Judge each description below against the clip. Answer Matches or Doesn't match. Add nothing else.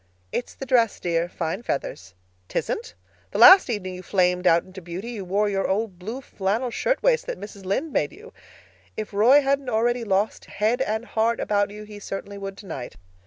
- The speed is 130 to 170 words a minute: Doesn't match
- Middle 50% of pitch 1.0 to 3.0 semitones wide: Doesn't match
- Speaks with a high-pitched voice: Matches